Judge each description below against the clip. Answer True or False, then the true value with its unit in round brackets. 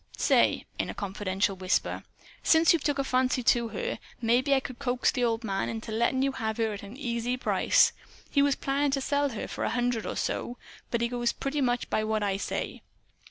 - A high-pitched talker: True (245 Hz)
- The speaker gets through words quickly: True (215 wpm)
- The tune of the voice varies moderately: True (3.7 semitones)